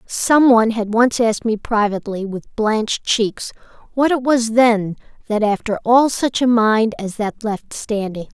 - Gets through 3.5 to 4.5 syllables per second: Yes, 4.4 syllables/s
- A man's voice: No, female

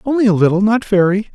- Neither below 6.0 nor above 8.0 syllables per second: Yes, 6.8 syllables/s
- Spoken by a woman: No, male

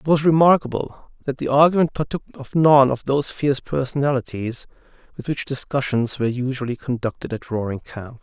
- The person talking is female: No, male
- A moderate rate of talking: Yes, average, 160 wpm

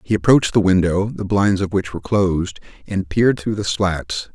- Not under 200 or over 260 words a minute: Yes, fast, 205 wpm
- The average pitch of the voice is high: No, very low, 95 Hz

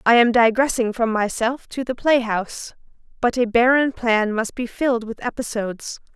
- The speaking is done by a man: No, female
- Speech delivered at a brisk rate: No, average, 175 wpm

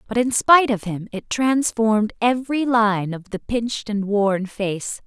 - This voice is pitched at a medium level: No, high, 220 Hz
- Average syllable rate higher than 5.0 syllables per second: No, 4.5 syllables/s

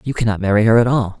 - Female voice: No, male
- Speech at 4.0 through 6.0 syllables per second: No, 7.4 syllables/s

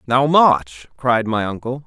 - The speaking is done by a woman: No, male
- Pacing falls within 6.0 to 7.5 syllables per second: No, 3.7 syllables/s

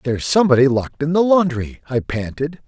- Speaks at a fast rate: No, average, 180 wpm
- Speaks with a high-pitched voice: No, medium, 145 Hz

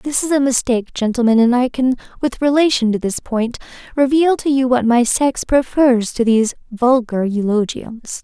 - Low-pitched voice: No, high, 245 Hz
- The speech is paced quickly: No, average, 175 wpm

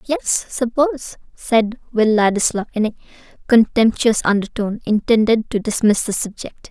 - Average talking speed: No, slow, 125 wpm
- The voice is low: No, high, 225 Hz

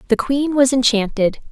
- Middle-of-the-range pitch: No, very high, 250 Hz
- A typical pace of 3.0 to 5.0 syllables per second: Yes, 4.9 syllables/s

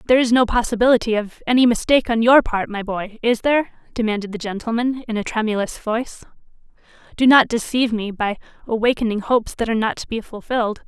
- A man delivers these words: No, female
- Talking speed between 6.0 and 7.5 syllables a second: Yes, 6.6 syllables/s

